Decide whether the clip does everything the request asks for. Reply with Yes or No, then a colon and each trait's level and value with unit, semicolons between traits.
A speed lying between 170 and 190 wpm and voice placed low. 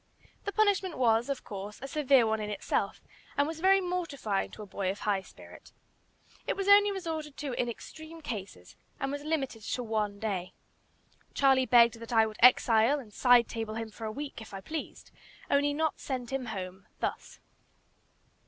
No: average, 180 wpm; high, 245 Hz